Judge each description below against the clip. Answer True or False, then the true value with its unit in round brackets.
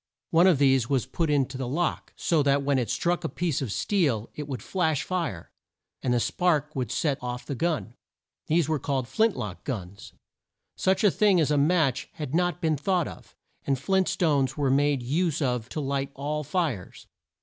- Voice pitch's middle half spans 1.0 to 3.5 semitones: False (4.5 semitones)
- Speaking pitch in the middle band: True (145 Hz)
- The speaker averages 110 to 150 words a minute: False (195 wpm)